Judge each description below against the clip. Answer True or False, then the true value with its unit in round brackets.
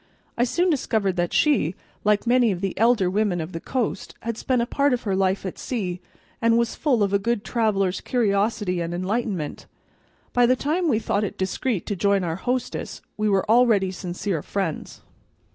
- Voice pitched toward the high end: True (210 Hz)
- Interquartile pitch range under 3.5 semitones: False (4.1 semitones)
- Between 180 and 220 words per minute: True (190 wpm)